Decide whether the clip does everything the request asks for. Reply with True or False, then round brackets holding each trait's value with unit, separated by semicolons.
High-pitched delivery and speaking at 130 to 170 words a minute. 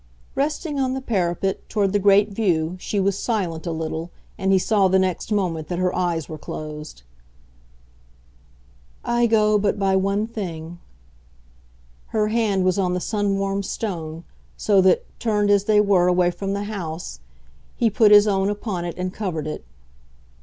True (195 Hz; 165 wpm)